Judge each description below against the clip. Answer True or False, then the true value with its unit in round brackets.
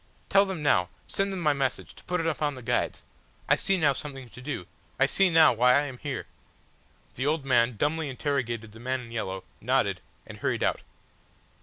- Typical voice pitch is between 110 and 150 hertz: True (135 Hz)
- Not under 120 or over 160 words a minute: False (200 wpm)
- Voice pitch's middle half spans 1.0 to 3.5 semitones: False (4.1 semitones)